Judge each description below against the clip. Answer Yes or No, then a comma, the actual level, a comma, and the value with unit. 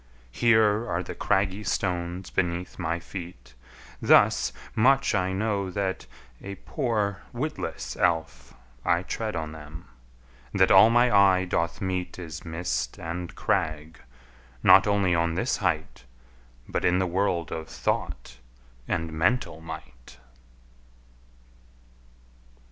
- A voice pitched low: Yes, very low, 90 Hz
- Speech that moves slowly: Yes, slow, 120 wpm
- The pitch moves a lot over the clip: No, average, 3.3 semitones